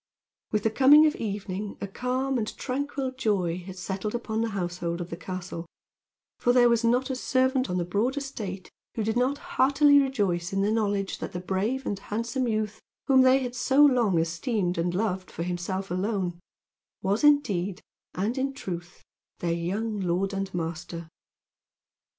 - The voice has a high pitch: Yes, high, 210 Hz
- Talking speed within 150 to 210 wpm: Yes, average, 170 wpm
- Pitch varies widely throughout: Yes, wide, 6.0 semitones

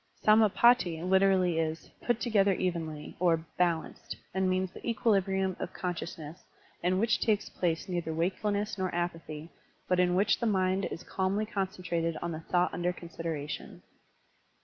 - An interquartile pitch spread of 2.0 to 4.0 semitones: Yes, average, 2.7 semitones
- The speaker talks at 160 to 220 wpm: No, average, 145 wpm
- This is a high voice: No, medium, 180 Hz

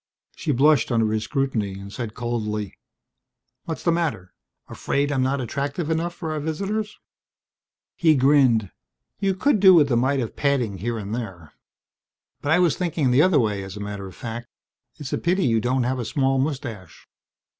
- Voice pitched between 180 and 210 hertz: No, low, 130 Hz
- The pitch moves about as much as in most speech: No, wide, 5.8 semitones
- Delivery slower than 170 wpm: No, average, 175 wpm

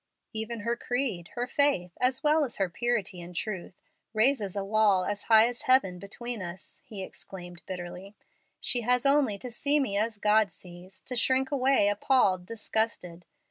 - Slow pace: No, average, 170 wpm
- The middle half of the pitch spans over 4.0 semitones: Yes, average, 4.7 semitones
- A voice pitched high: Yes, high, 215 Hz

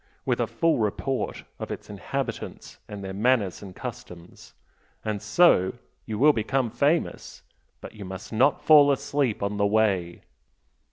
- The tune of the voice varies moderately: No, wide, 5.7 semitones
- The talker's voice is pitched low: Yes, low, 110 Hz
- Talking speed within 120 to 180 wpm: Yes, average, 150 wpm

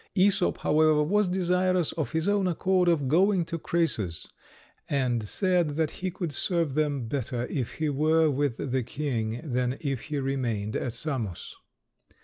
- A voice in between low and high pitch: Yes, medium, 150 Hz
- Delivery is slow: No, average, 155 wpm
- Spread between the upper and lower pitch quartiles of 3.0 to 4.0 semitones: No, average, 5.3 semitones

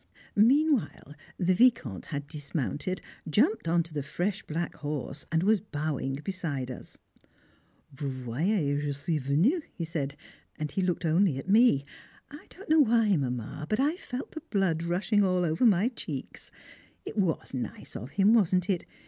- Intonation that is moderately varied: No, wide, 6.4 semitones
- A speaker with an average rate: Yes, average, 165 wpm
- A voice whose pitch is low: No, medium, 170 Hz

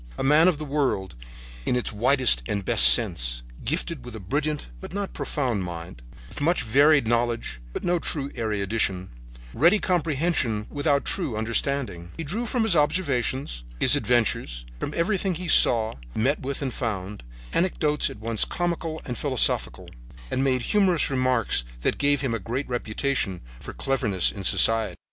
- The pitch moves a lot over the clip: Yes, wide, 6.0 semitones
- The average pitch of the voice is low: Yes, low, 130 Hz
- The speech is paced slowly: No, average, 160 wpm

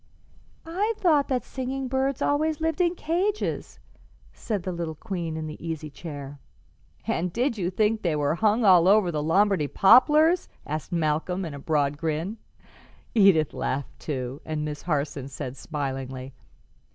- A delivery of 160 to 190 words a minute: No, average, 150 wpm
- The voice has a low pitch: No, medium, 175 Hz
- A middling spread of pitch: No, wide, 8.6 semitones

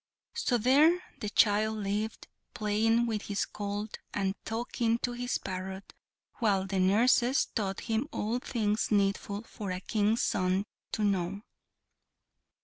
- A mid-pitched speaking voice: No, high, 210 Hz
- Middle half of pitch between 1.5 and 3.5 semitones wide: Yes, narrow, 2.6 semitones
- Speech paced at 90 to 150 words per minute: Yes, slow, 135 wpm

